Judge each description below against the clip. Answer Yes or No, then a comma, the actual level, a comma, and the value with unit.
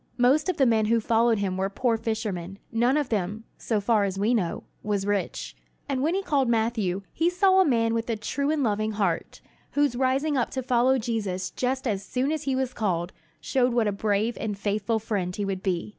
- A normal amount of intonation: Yes, average, 4.3 semitones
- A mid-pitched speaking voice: No, high, 225 Hz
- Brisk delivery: Yes, fast, 220 wpm